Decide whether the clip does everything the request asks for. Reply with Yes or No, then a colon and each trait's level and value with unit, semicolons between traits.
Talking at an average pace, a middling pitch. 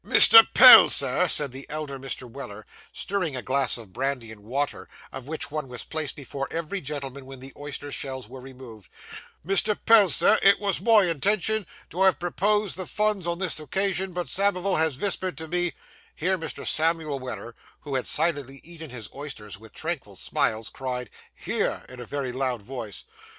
Yes: average, 180 wpm; medium, 145 Hz